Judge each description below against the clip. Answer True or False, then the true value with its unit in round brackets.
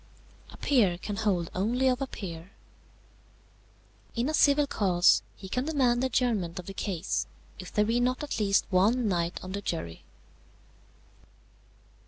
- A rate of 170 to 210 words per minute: False (155 wpm)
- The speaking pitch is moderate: False (210 Hz)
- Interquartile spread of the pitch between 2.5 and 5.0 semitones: False (5.5 semitones)